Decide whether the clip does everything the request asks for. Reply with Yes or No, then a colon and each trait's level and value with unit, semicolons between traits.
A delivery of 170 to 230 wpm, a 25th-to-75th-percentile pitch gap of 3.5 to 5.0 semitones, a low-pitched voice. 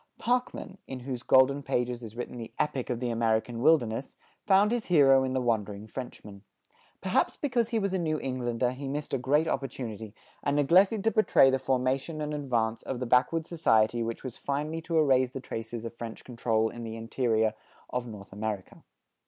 Yes: average, 185 wpm; average, 4.6 semitones; low, 130 Hz